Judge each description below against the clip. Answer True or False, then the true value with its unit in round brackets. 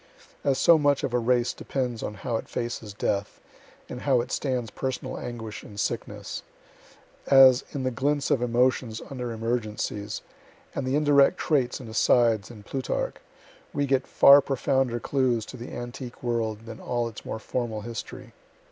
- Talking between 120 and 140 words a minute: False (165 wpm)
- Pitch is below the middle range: True (125 Hz)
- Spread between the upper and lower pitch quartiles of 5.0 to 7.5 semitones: False (2.6 semitones)